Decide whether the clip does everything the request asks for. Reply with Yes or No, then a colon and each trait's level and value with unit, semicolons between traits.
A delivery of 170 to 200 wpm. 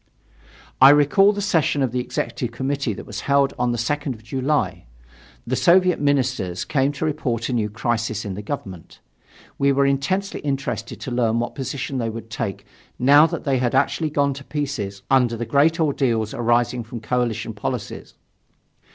Yes: average, 175 wpm